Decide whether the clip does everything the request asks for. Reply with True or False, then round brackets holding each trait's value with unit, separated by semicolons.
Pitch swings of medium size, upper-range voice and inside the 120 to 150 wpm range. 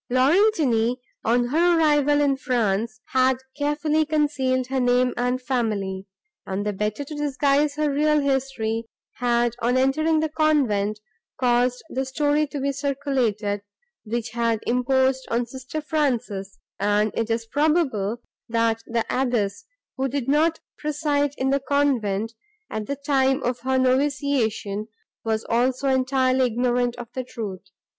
True (3.8 semitones; 255 Hz; 140 wpm)